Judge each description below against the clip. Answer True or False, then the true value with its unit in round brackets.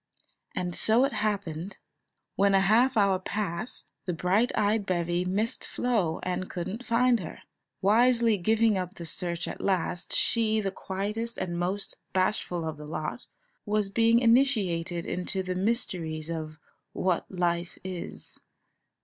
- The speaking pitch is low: False (190 Hz)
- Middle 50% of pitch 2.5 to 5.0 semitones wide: True (4.0 semitones)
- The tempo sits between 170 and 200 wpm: False (145 wpm)